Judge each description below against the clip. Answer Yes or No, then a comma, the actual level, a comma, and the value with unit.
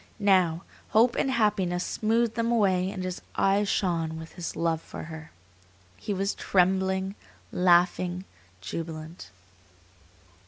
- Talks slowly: Yes, slow, 120 wpm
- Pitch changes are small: No, average, 3.1 semitones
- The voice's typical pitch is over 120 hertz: Yes, medium, 185 Hz